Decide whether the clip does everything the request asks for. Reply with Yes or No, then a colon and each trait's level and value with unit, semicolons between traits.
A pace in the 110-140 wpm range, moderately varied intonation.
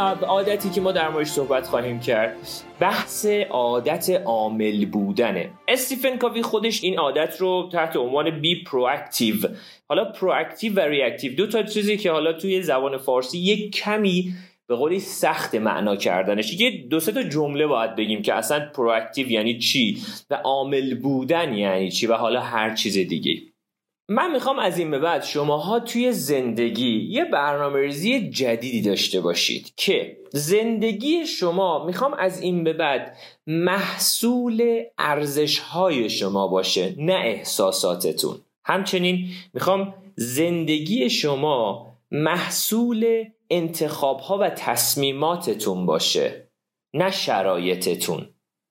No: average, 130 wpm; wide, 7.2 semitones